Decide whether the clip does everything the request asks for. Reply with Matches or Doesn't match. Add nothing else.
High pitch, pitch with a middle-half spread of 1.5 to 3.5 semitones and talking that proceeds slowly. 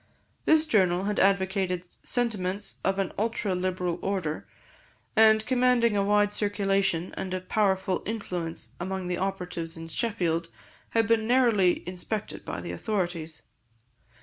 Matches